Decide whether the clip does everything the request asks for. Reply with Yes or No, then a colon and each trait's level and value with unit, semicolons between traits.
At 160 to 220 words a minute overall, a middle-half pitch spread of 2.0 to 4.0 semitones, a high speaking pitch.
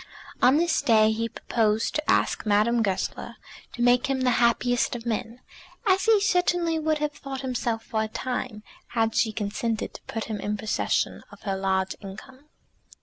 Yes: average, 175 wpm; average, 3.7 semitones; high, 235 Hz